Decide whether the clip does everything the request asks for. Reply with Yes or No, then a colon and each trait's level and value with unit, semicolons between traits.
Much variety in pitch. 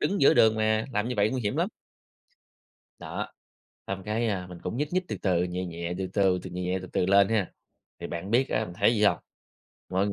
No: average, 3.3 semitones